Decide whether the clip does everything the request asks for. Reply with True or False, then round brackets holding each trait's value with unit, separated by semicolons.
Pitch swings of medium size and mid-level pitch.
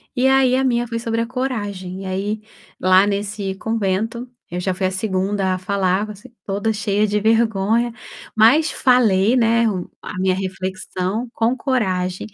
False (3.5 semitones; 210 Hz)